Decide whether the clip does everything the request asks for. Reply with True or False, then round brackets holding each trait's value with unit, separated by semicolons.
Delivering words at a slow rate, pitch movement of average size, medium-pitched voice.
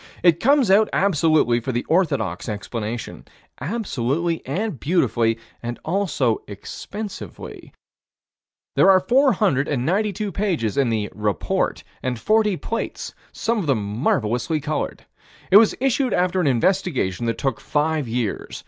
False (120 wpm; 8.7 semitones; 155 Hz)